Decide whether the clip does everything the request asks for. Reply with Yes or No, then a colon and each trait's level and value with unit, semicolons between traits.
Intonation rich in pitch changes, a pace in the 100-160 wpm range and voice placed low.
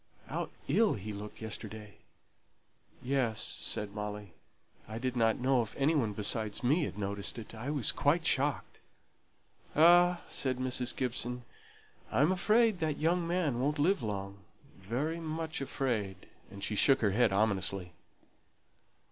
Yes: wide, 6.3 semitones; average, 140 wpm; low, 125 Hz